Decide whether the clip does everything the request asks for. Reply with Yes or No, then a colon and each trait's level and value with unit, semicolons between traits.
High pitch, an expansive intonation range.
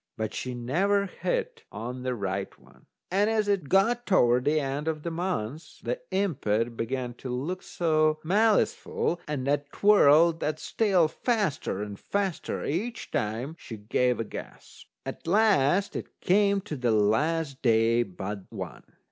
No: medium, 150 Hz; wide, 8.1 semitones